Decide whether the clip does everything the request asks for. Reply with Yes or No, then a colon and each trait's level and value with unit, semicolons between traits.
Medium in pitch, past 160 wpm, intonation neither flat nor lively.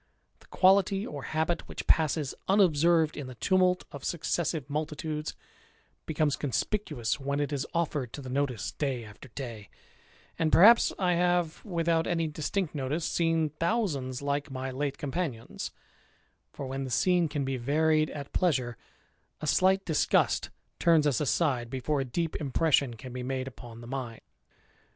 No: medium, 150 Hz; average, 155 wpm; average, 4.1 semitones